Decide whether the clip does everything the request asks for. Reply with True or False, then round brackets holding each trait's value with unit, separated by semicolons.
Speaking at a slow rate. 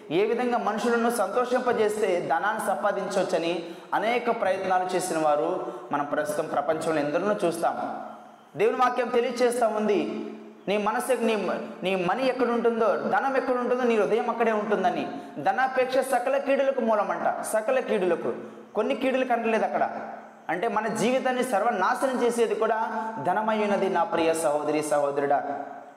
False (120 wpm)